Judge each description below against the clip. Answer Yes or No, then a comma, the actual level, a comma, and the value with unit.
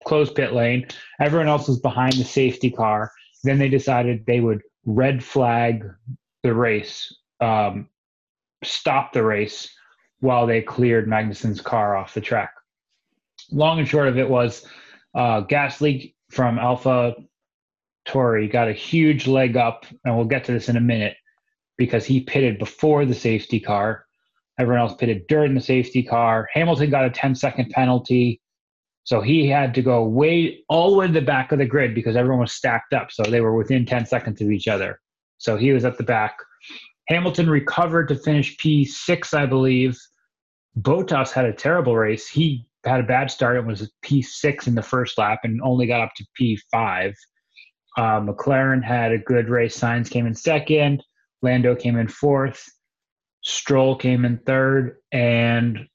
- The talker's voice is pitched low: Yes, low, 125 Hz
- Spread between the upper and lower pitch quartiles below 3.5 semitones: Yes, average, 3.0 semitones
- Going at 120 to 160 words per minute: No, average, 175 wpm